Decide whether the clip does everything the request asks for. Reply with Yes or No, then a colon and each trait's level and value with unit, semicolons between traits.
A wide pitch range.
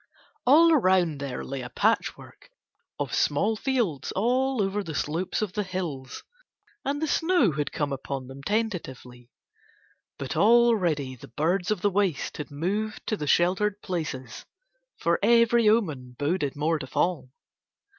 Yes: wide, 7.2 semitones